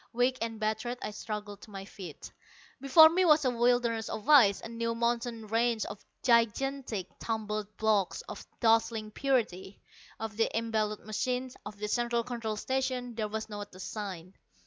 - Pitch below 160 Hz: No, high, 225 Hz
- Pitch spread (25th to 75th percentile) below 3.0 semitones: Yes, narrow, 2.4 semitones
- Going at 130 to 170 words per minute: Yes, average, 165 wpm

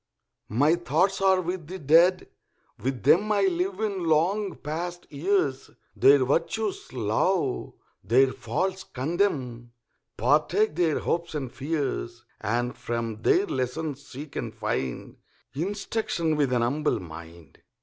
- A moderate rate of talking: No, slow, 125 wpm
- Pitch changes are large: Yes, wide, 6.6 semitones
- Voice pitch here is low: No, medium, 155 Hz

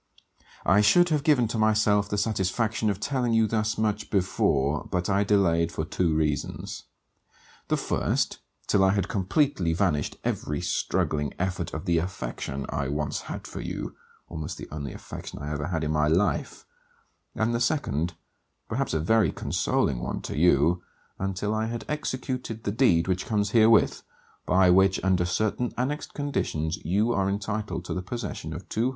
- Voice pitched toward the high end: No, very low, 95 Hz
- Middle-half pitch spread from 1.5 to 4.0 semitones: No, average, 5.0 semitones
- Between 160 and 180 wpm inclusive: Yes, average, 170 wpm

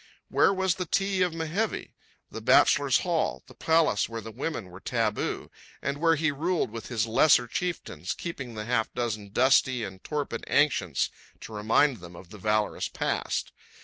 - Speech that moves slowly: No, average, 165 wpm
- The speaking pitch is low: Yes, low, 125 Hz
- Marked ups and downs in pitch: Yes, wide, 7.0 semitones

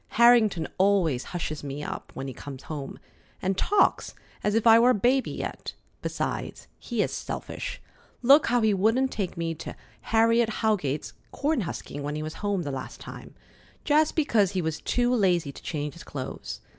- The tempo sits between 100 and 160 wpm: No, average, 180 wpm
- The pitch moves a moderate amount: No, wide, 7.3 semitones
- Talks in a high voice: Yes, high, 195 Hz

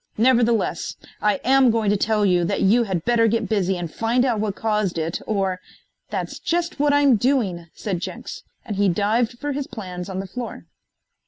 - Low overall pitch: No, high, 215 Hz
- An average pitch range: Yes, average, 4.1 semitones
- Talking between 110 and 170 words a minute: No, average, 195 wpm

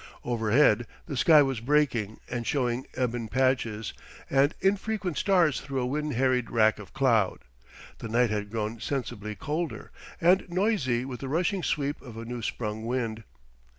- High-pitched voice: No, low, 125 Hz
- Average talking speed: Yes, average, 155 wpm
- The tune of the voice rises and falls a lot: No, average, 4.6 semitones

